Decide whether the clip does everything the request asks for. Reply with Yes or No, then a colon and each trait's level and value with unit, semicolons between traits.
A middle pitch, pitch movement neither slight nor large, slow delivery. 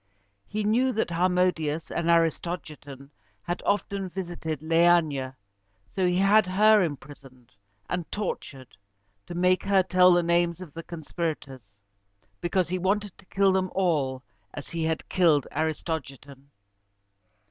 Yes: medium, 170 Hz; average, 3.6 semitones; slow, 130 wpm